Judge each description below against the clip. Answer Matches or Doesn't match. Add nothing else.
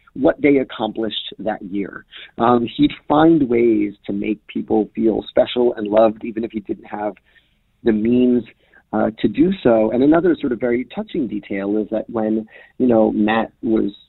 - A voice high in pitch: Doesn't match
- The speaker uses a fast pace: Doesn't match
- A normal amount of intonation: Doesn't match